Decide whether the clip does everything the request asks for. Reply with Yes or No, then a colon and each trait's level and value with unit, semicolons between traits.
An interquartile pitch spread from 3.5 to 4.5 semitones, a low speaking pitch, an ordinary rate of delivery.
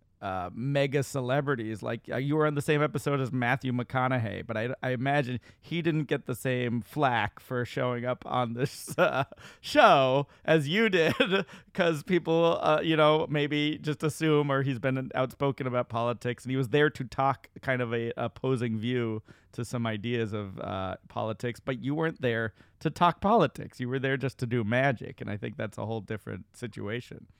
Yes: average, 3.8 semitones; low, 130 Hz; average, 190 wpm